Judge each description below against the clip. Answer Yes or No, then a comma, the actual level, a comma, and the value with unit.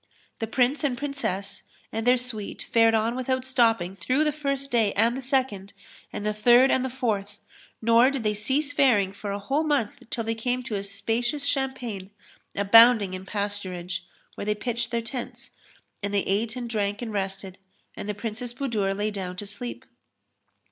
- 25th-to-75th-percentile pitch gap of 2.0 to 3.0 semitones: No, average, 4.0 semitones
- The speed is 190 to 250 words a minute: No, average, 180 wpm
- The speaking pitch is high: Yes, high, 225 Hz